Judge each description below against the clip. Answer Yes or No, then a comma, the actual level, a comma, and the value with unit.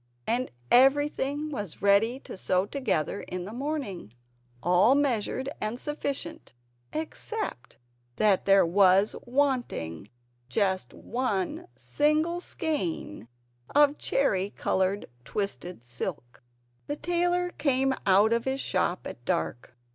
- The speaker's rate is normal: No, slow, 110 wpm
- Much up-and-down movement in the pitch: Yes, wide, 7.4 semitones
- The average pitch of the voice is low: No, high, 230 Hz